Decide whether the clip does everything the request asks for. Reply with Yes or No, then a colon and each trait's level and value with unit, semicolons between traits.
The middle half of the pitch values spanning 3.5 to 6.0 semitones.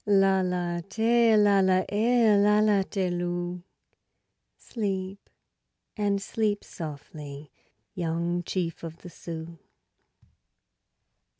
No: average, 3.1 semitones